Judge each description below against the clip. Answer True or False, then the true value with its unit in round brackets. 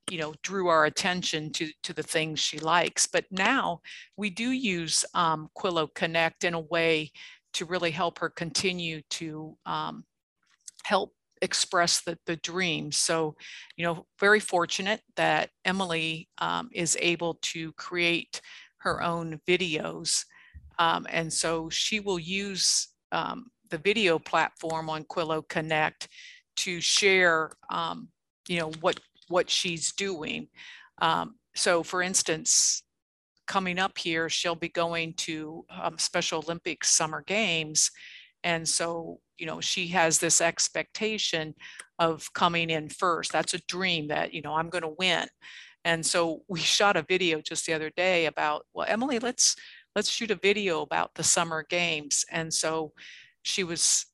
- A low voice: False (170 Hz)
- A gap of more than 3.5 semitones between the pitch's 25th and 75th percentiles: False (2.8 semitones)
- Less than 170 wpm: True (150 wpm)